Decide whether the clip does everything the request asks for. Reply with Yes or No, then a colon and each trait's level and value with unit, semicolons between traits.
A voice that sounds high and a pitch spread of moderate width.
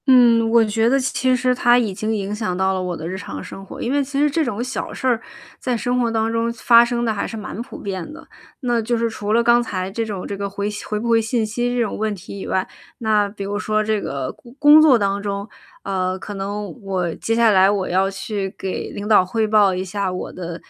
Yes: high, 215 Hz; average, 3.2 semitones